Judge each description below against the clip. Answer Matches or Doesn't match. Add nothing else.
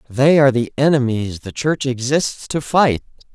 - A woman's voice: Doesn't match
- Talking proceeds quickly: Doesn't match